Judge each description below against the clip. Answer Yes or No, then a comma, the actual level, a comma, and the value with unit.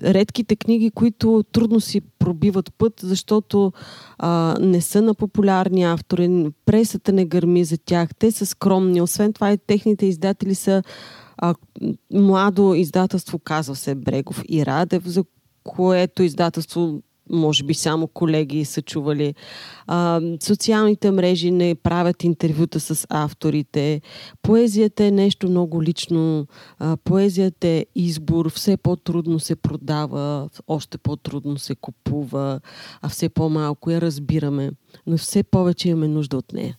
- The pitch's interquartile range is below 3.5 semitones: No, average, 3.9 semitones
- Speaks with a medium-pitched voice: Yes, medium, 175 Hz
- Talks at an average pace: Yes, average, 130 wpm